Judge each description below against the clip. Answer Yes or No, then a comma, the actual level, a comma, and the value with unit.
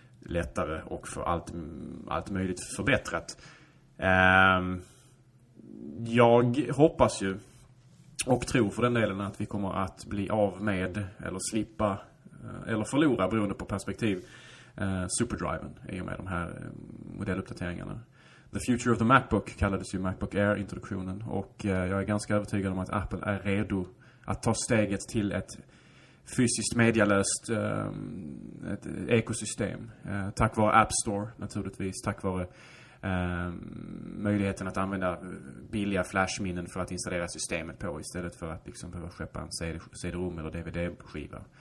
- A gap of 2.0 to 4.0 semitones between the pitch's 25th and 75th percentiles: Yes, average, 3.5 semitones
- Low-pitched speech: Yes, low, 100 Hz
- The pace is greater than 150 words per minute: No, average, 135 wpm